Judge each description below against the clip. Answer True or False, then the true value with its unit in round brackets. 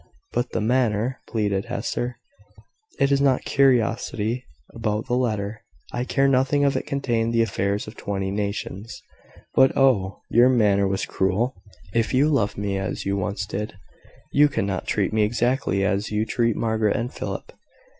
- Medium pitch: False (115 Hz)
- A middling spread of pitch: True (3.8 semitones)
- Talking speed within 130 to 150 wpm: False (165 wpm)